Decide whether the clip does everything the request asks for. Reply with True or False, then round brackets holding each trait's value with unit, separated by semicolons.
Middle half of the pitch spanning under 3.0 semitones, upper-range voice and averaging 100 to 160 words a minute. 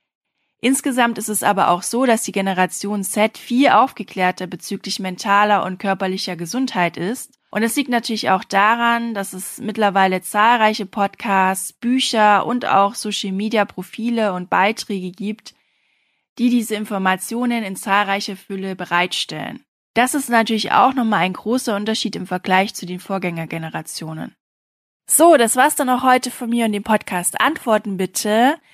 False (3.7 semitones; 210 Hz; 150 wpm)